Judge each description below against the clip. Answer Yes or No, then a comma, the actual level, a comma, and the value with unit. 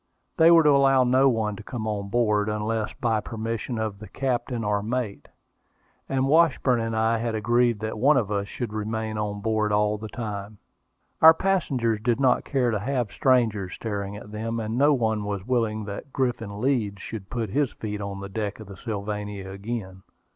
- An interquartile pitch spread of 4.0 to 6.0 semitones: No, average, 2.9 semitones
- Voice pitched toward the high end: No, low, 110 Hz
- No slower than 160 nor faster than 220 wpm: Yes, average, 190 wpm